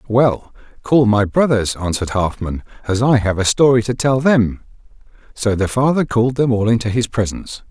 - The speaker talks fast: No, average, 180 wpm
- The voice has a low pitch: Yes, low, 115 Hz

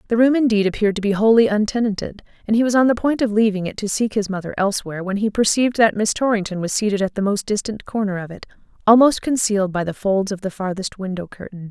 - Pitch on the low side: No, high, 210 Hz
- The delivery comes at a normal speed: No, fast, 240 wpm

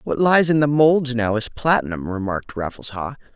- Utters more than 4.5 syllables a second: Yes, 5.2 syllables/s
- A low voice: Yes, low, 125 Hz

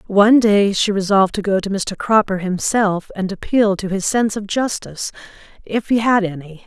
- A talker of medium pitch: No, high, 200 Hz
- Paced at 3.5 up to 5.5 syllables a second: Yes, 5.2 syllables/s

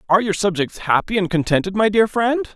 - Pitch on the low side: No, high, 200 Hz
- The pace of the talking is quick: Yes, fast, 210 wpm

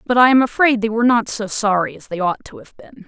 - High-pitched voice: Yes, high, 225 Hz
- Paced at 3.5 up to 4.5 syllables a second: No, 6.3 syllables/s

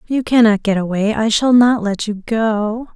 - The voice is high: Yes, high, 220 Hz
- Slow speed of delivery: No, fast, 205 wpm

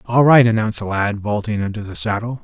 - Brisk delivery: Yes, fast, 220 wpm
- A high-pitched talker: No, low, 110 Hz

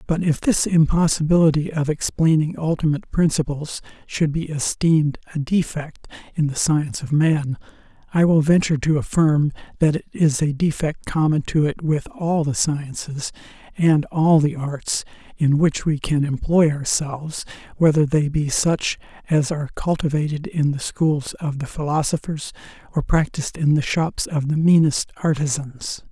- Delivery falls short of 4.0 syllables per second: No, 4.7 syllables/s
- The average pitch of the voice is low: No, medium, 150 Hz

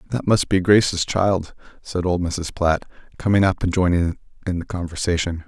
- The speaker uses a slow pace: No, average, 175 wpm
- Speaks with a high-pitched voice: No, very low, 90 Hz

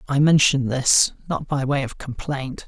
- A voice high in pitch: No, low, 135 Hz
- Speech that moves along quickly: No, average, 180 wpm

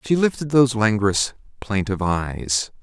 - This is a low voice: Yes, low, 110 Hz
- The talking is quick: No, slow, 125 wpm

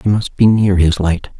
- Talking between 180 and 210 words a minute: No, fast, 255 wpm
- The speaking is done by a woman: No, male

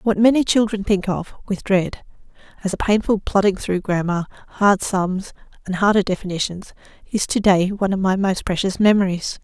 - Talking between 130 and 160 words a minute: No, average, 170 wpm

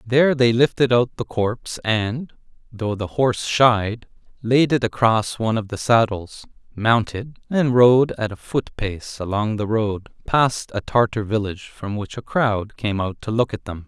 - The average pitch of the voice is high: No, low, 115 Hz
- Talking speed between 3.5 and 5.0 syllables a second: Yes, 4.2 syllables/s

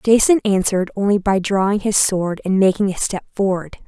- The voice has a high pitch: Yes, high, 195 Hz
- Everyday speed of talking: Yes, average, 185 wpm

